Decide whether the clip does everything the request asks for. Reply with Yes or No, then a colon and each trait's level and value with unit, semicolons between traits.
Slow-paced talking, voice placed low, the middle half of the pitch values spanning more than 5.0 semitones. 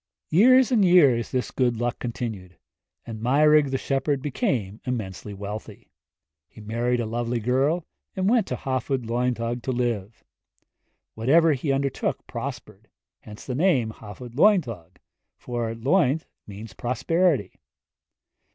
No: slow, 130 wpm; low, 125 Hz; average, 4.3 semitones